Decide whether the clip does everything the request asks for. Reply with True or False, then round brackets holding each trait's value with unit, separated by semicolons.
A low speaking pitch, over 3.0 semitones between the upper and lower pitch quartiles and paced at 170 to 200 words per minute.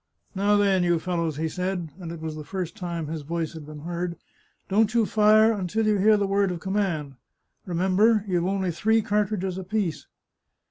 False (185 Hz; 3.5 semitones; 195 wpm)